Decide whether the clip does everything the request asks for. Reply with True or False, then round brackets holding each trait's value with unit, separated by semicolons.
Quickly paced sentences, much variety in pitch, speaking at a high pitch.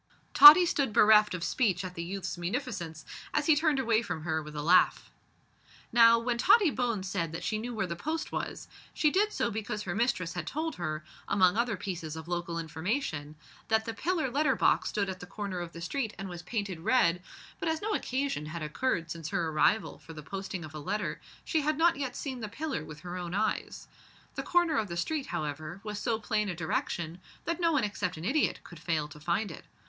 True (220 wpm; 6.9 semitones; 200 Hz)